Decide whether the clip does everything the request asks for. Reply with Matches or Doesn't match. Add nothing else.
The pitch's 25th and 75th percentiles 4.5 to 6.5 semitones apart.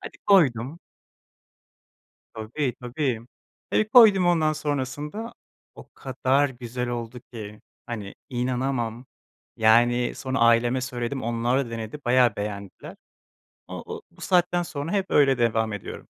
Doesn't match